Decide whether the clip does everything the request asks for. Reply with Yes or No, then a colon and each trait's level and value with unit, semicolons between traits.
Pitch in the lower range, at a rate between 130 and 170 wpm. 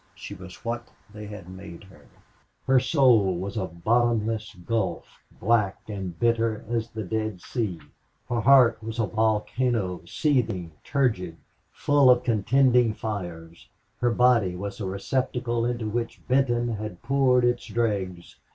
Yes: low, 110 Hz; average, 140 wpm